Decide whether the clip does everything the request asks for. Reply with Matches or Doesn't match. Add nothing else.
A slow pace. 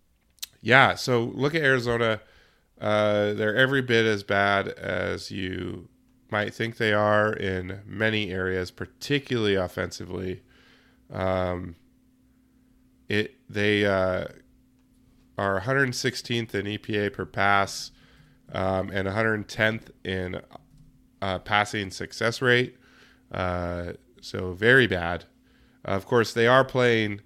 Matches